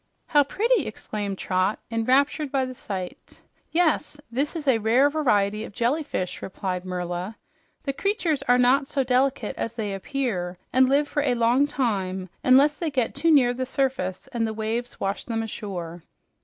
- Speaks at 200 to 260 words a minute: No, average, 170 wpm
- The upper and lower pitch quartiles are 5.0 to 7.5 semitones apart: Yes, wide, 5.5 semitones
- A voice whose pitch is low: No, high, 245 Hz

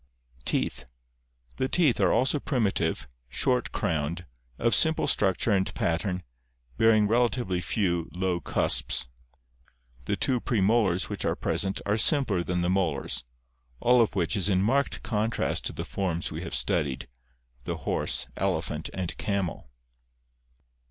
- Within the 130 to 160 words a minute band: Yes, average, 140 wpm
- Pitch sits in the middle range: No, very low, 95 Hz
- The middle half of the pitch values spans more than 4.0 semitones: Yes, average, 5.2 semitones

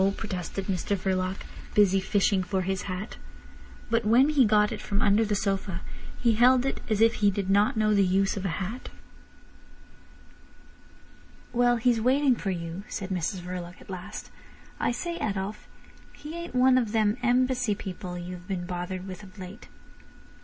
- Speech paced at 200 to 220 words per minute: No, average, 165 wpm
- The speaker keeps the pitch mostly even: No, average, 3.8 semitones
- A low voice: No, high, 200 Hz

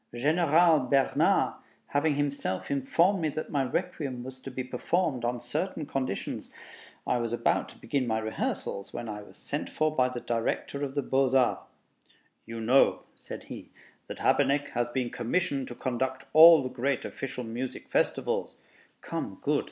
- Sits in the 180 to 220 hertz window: No, low, 130 Hz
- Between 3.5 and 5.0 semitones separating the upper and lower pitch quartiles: No, average, 3.0 semitones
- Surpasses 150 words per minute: Yes, average, 165 wpm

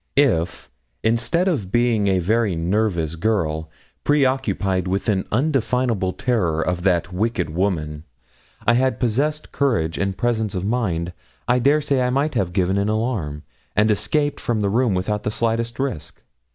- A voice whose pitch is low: Yes, low, 105 Hz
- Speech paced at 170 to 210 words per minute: No, average, 155 wpm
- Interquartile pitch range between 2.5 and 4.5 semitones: No, average, 5.3 semitones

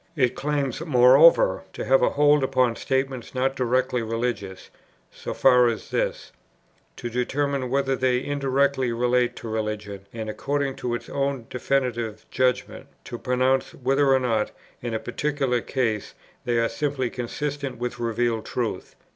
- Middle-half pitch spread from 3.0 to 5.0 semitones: No, narrow, 2.6 semitones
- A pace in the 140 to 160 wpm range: Yes, average, 145 wpm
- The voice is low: Yes, low, 125 Hz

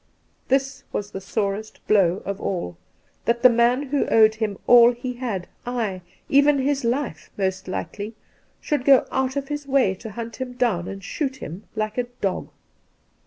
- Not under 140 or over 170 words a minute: No, average, 180 wpm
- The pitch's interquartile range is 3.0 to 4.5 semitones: No, average, 4.9 semitones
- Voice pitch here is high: Yes, high, 235 Hz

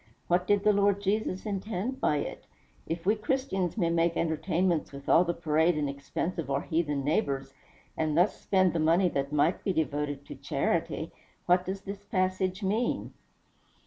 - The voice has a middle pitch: Yes, medium, 175 Hz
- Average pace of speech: Yes, average, 175 wpm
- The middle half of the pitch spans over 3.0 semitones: Yes, average, 4.1 semitones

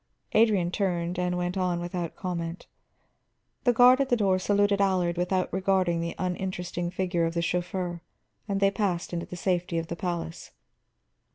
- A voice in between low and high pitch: Yes, medium, 180 Hz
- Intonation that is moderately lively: No, narrow, 1.9 semitones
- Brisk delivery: No, average, 165 wpm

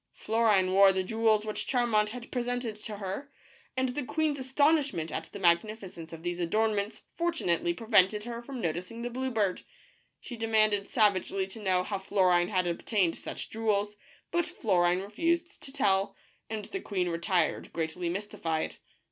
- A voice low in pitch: No, high, 210 Hz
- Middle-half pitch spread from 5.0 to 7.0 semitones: No, average, 4.4 semitones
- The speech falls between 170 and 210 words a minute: No, average, 160 wpm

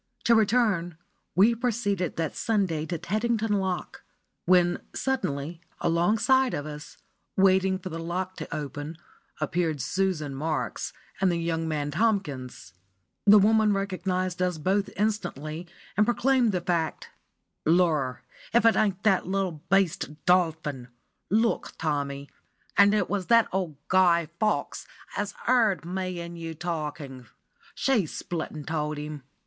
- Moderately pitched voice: Yes, medium, 180 Hz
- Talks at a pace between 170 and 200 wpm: No, slow, 135 wpm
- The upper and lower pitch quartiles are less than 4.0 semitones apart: No, average, 4.4 semitones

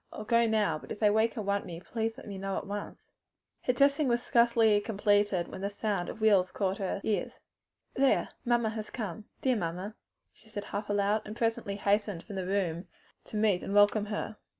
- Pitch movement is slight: Yes, narrow, 2.0 semitones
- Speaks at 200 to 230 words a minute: Yes, fast, 205 wpm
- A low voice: No, high, 210 Hz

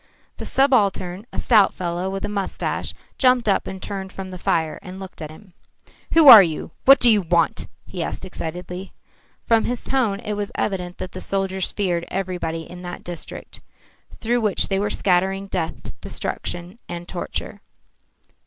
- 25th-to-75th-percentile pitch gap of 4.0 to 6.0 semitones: No, average, 2.8 semitones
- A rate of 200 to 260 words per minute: No, average, 165 wpm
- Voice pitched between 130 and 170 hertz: No, high, 190 Hz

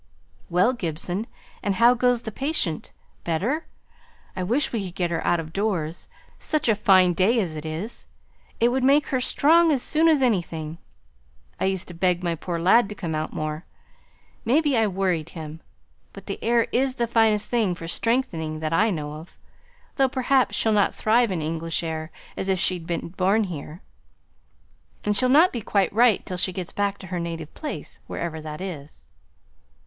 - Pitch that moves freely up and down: Yes, wide, 6.1 semitones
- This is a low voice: No, high, 190 Hz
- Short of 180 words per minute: No, average, 185 wpm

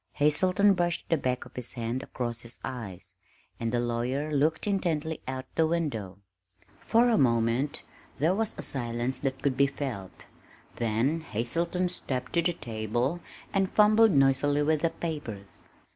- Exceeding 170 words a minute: No, average, 155 wpm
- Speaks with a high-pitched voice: No, medium, 140 Hz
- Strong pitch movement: Yes, wide, 5.8 semitones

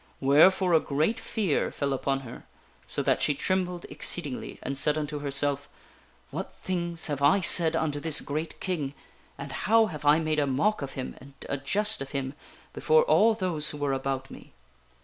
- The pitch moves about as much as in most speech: Yes, average, 4.4 semitones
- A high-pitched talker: No, medium, 150 Hz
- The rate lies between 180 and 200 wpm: Yes, average, 190 wpm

